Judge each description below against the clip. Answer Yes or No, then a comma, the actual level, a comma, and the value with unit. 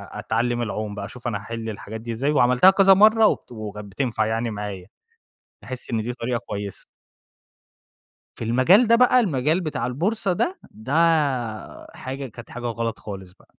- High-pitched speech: No, low, 120 Hz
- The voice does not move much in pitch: No, average, 5.3 semitones